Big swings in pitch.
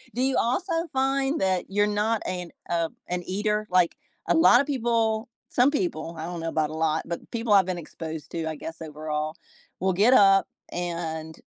Yes: wide, 5.9 semitones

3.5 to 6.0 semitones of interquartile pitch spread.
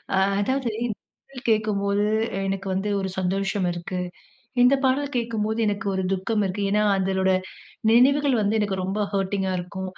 No: average, 3.1 semitones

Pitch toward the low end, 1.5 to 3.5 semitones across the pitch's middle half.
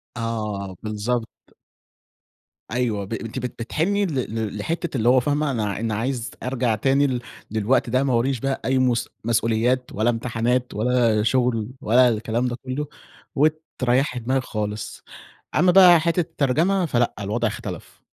Yes: low, 125 Hz; average, 3.0 semitones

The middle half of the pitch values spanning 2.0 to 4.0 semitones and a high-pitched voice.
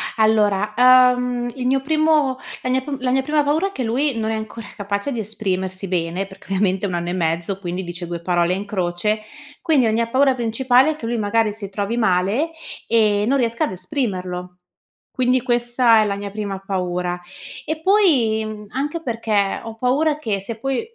No: average, 4.8 semitones; high, 220 Hz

